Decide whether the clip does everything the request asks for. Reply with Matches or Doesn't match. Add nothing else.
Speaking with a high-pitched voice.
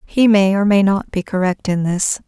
Matches